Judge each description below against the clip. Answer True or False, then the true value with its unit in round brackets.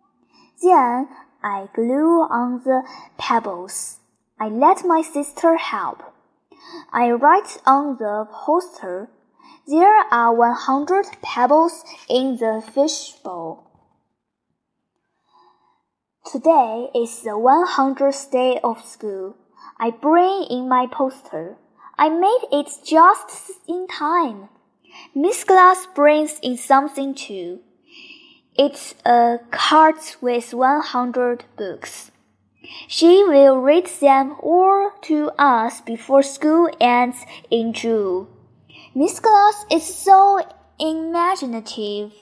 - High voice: True (280 Hz)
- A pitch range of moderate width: False (5.8 semitones)